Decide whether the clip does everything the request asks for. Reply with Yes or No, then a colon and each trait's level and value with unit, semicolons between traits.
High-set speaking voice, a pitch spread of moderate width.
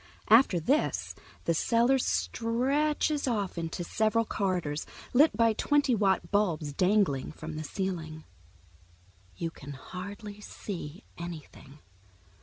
No: high, 195 Hz; wide, 5.9 semitones